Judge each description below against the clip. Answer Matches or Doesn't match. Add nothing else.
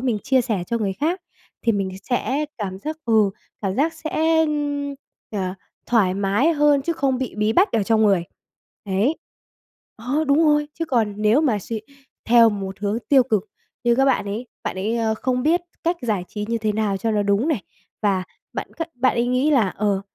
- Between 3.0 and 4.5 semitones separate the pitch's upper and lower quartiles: Doesn't match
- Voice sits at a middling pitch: Doesn't match